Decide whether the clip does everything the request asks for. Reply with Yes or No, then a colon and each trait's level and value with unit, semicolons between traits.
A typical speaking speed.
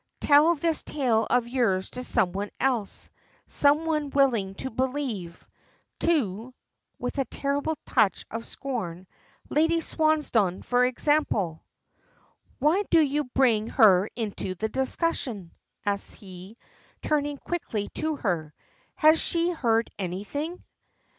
No: slow, 120 wpm